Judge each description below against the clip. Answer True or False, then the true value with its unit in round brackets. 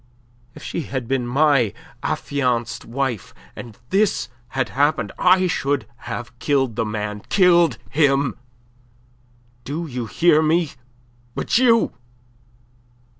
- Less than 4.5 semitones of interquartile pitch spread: False (5.2 semitones)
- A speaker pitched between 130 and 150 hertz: True (140 Hz)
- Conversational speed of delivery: False (115 wpm)